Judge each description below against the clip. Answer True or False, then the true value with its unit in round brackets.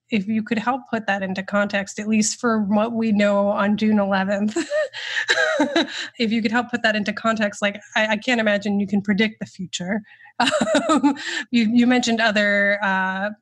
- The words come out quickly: False (180 wpm)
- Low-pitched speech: False (215 Hz)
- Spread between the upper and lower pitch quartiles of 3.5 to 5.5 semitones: False (2.7 semitones)